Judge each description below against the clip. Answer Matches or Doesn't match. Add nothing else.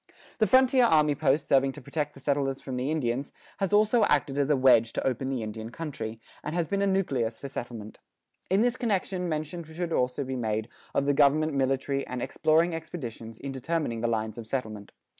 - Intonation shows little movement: Doesn't match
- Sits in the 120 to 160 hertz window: Matches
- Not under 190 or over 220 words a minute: Matches